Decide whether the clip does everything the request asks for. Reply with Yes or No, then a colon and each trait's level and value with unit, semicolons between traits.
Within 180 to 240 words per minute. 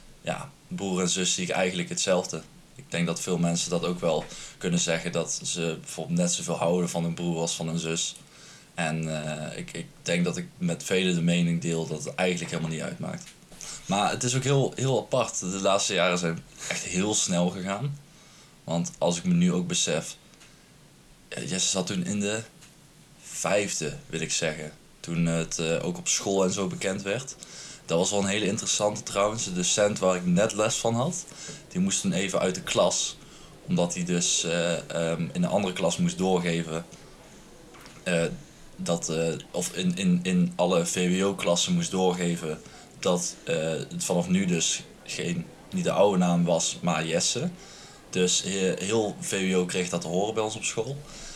Yes: average, 190 wpm